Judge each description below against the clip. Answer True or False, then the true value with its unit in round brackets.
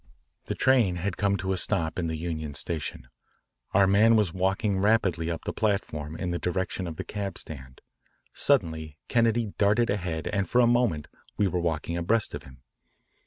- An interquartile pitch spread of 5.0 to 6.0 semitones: False (4.2 semitones)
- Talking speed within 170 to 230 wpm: True (180 wpm)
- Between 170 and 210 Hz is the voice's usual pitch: False (95 Hz)